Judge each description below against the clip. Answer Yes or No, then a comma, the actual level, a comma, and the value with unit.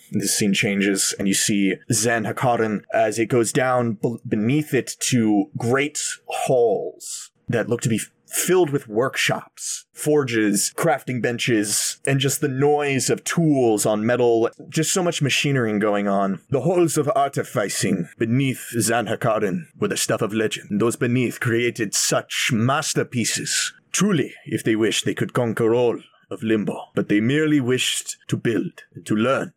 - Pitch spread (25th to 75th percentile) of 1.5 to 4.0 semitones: No, average, 4.6 semitones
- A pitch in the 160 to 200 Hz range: No, low, 120 Hz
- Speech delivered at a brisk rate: No, average, 160 wpm